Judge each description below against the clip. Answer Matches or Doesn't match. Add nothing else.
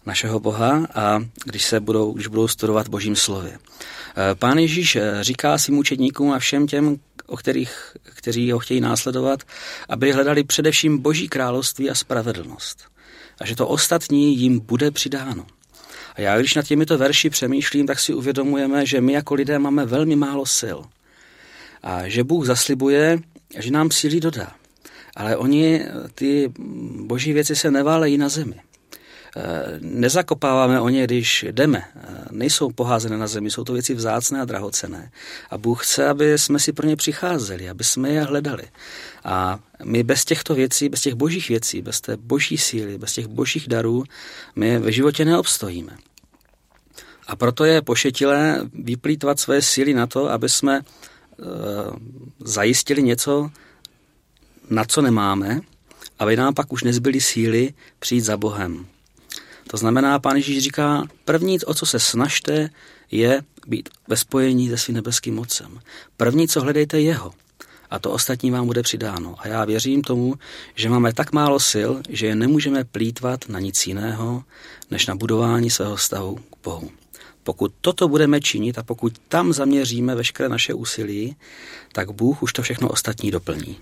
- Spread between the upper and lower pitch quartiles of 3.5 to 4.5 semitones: Matches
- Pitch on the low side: Matches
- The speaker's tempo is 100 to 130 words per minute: Doesn't match